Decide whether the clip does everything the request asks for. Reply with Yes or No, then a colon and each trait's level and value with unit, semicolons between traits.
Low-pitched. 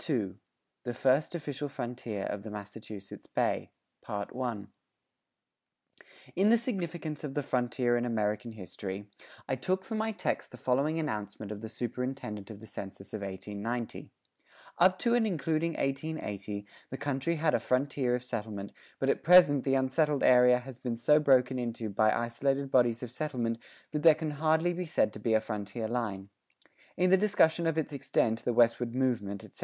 Yes: low, 125 Hz